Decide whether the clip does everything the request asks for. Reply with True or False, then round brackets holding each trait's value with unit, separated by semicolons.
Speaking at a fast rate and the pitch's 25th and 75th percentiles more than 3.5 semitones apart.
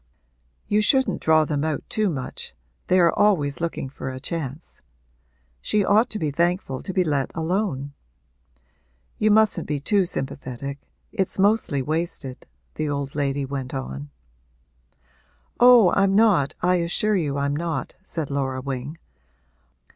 False (140 wpm; 5.6 semitones)